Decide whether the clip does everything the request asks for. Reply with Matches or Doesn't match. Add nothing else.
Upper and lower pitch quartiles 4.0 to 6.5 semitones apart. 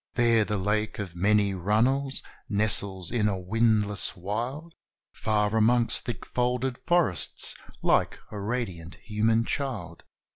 Doesn't match